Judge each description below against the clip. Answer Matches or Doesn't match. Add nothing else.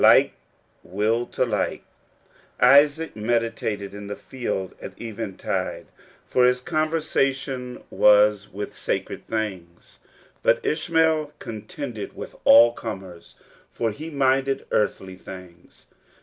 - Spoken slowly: Matches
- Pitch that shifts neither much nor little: Matches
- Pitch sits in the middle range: Doesn't match